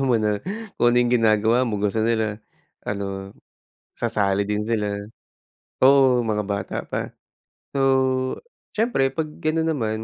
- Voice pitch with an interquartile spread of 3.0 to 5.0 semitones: Yes, average, 3.7 semitones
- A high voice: No, low, 110 Hz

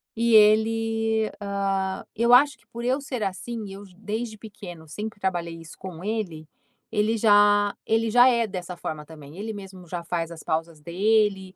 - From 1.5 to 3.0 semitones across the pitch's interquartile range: No, average, 4.0 semitones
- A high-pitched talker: Yes, high, 205 Hz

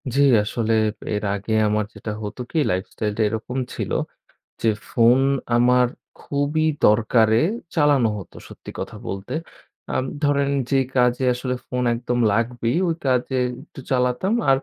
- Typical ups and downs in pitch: Yes, average, 3.1 semitones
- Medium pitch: No, low, 125 Hz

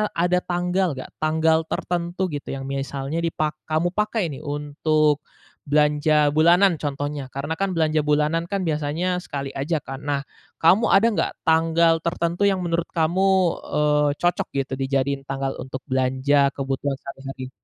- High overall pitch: No, medium, 155 Hz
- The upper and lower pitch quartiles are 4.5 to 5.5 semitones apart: No, average, 3.4 semitones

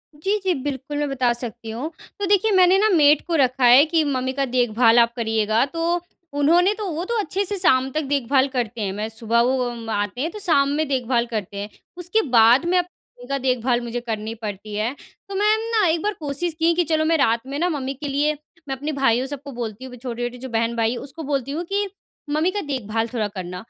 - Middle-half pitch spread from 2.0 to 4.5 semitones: No, wide, 5.5 semitones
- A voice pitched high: Yes, very high, 265 Hz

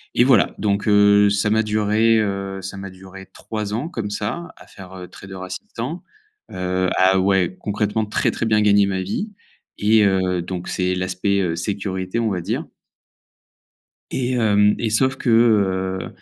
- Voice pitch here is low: Yes, low, 100 Hz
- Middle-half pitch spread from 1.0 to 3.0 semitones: Yes, narrow, 2.5 semitones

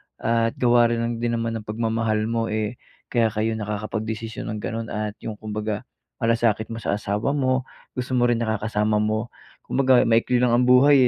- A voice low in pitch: Yes, low, 115 Hz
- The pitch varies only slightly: Yes, narrow, 1.7 semitones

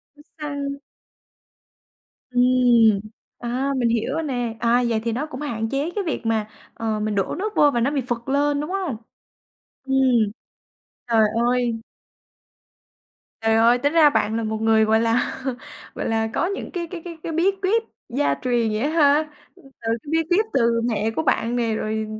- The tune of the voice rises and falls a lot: No, average, 4.5 semitones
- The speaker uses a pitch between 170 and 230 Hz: No, high, 245 Hz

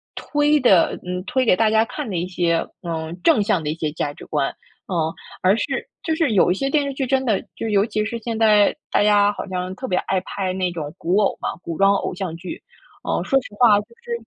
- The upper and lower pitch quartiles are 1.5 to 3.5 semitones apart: No, average, 4.7 semitones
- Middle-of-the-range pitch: No, high, 200 Hz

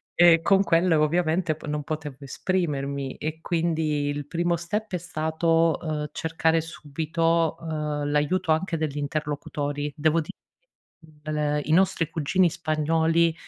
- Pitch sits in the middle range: Yes, medium, 160 Hz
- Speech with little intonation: Yes, narrow, 2.0 semitones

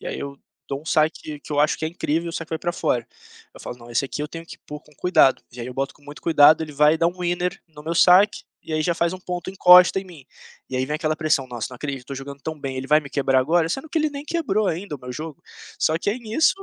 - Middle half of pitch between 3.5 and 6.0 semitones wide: Yes, average, 3.9 semitones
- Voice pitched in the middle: Yes, medium, 155 Hz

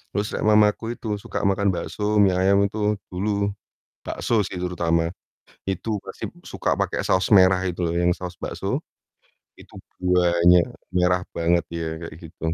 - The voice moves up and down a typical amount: No, narrow, 2.0 semitones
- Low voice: Yes, very low, 90 Hz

